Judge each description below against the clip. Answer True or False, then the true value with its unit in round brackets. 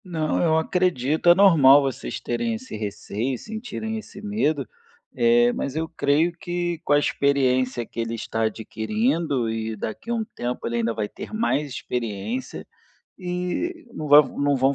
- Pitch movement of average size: False (6.8 semitones)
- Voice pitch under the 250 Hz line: True (140 Hz)